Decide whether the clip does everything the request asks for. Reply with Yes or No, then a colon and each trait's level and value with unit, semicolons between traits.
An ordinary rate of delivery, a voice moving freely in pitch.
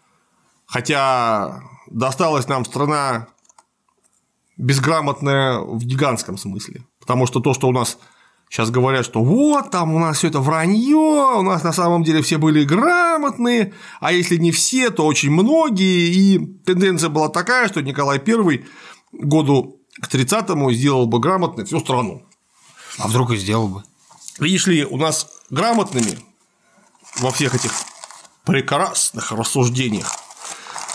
Yes: average, 130 wpm; wide, 6.2 semitones